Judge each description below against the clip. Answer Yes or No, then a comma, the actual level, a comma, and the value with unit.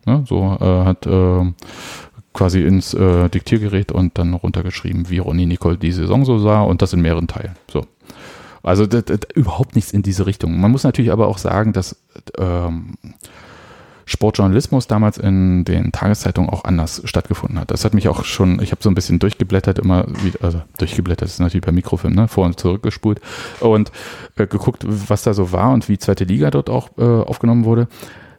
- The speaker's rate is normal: No, fast, 195 wpm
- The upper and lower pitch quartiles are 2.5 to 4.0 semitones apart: Yes, average, 3.4 semitones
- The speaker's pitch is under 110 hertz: Yes, very low, 95 Hz